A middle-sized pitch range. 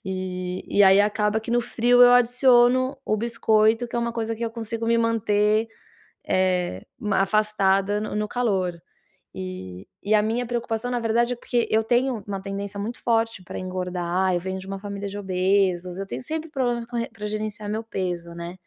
Yes: average, 3.5 semitones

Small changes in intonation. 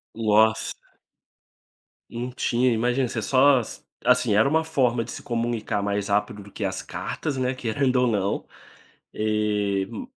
No: average, 3.4 semitones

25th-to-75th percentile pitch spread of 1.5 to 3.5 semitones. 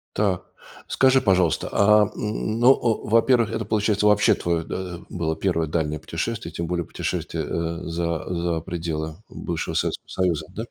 No: average, 4.1 semitones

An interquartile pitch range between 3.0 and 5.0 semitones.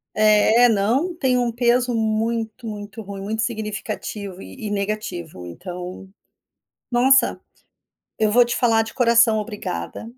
No: narrow, 2.6 semitones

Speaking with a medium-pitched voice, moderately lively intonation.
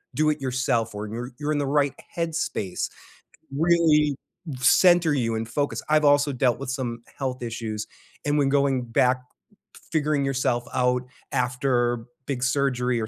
No: low, 130 Hz; average, 3.2 semitones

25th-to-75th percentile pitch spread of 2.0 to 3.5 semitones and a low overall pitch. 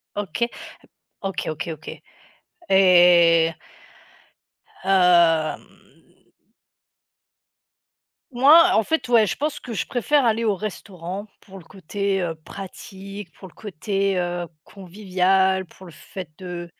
No: average, 2.8 semitones; high, 190 Hz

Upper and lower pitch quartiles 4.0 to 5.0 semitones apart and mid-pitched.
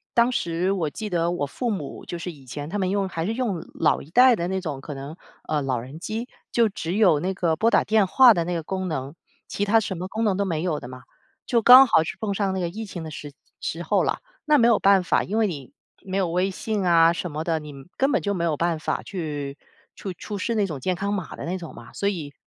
Yes: average, 4.3 semitones; medium, 180 Hz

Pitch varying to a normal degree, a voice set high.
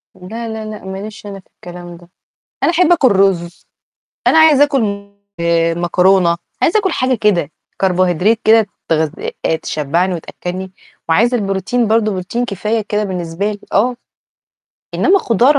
Yes: average, 4.4 semitones; high, 200 Hz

